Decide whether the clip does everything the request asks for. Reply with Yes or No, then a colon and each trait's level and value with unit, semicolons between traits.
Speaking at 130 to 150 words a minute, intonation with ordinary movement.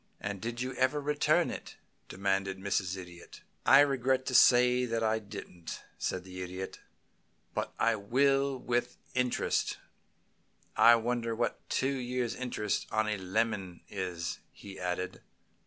Yes: average, 140 wpm; average, 4.7 semitones